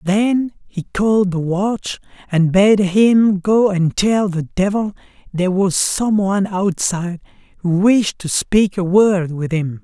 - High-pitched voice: Yes, high, 195 Hz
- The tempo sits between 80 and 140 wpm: No, average, 160 wpm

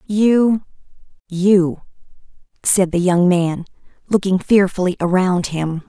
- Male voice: No, female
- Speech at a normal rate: No, slow, 90 wpm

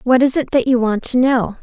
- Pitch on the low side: No, very high, 250 Hz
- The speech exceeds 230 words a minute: Yes, fast, 295 wpm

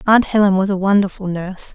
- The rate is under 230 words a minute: Yes, fast, 205 wpm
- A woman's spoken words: Yes, female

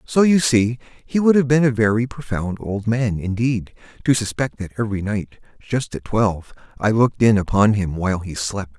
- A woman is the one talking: No, male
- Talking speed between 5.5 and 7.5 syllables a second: No, 5.1 syllables/s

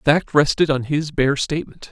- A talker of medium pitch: Yes, medium, 145 Hz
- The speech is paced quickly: Yes, fast, 220 wpm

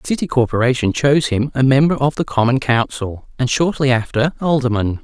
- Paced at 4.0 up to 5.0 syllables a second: No, 5.6 syllables/s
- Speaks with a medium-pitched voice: No, low, 130 Hz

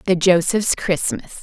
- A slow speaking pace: Yes, slow, 125 wpm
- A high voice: No, medium, 180 Hz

